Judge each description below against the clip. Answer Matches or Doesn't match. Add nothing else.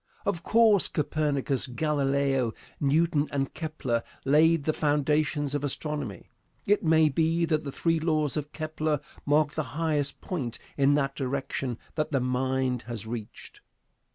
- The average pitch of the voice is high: Doesn't match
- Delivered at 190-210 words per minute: Doesn't match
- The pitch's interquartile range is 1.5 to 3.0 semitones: Matches